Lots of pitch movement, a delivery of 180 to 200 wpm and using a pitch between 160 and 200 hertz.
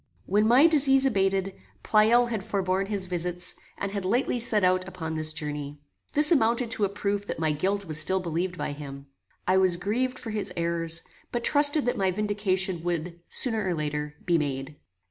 No: average, 4.5 semitones; average, 185 wpm; high, 190 Hz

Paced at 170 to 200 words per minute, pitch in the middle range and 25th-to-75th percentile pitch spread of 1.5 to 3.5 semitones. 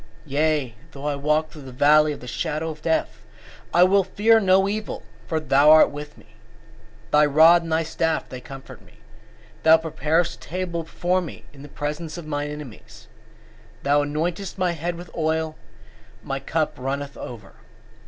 Yes: average, 180 wpm; medium, 155 Hz; average, 2.7 semitones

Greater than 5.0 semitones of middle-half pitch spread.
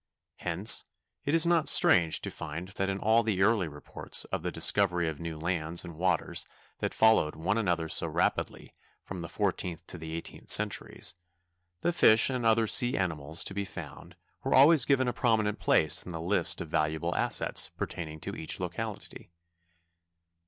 Yes: wide, 5.4 semitones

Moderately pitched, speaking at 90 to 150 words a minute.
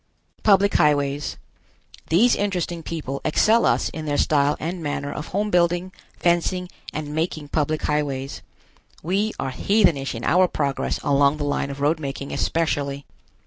Yes: medium, 155 Hz; average, 145 wpm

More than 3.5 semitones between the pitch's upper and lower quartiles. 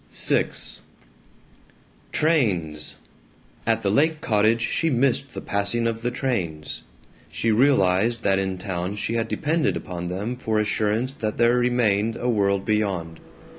Yes: average, 4.0 semitones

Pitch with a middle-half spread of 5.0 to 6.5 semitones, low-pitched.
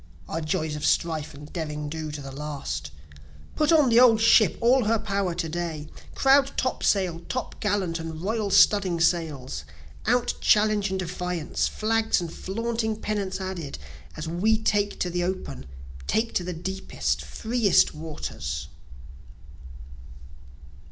No: wide, 5.4 semitones; medium, 185 Hz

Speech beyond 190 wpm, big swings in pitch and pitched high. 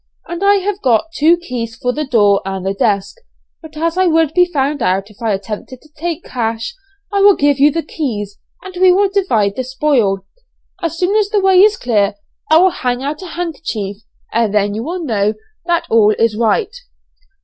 Yes: fast, 205 wpm; wide, 8.2 semitones; very high, 280 Hz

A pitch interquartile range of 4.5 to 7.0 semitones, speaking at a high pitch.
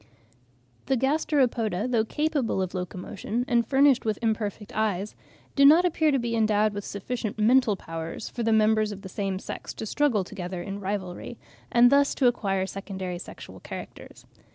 No: average, 4.1 semitones; high, 215 Hz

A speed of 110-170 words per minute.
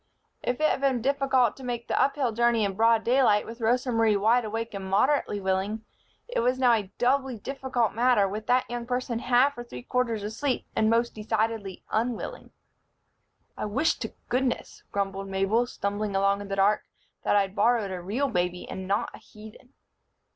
No: average, 185 wpm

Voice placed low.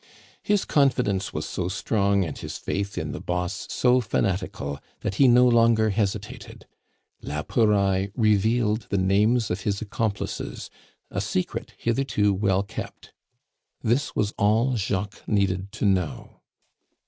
Yes: low, 100 Hz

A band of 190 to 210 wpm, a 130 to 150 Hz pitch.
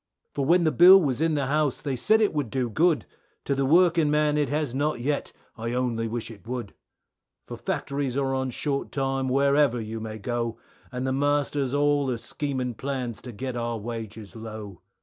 Yes: average, 195 wpm; low, 135 Hz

